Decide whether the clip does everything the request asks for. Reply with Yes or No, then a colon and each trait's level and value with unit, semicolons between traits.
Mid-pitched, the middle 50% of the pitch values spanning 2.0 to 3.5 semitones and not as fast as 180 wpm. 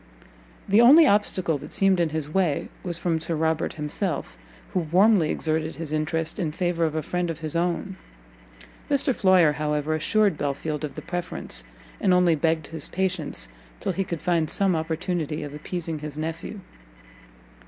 Yes: medium, 165 Hz; average, 2.9 semitones; average, 165 wpm